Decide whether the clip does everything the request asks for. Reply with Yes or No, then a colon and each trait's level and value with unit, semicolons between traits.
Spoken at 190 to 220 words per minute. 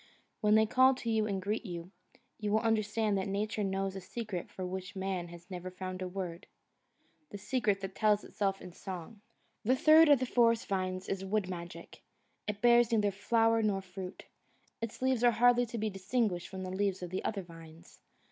Yes: average, 195 wpm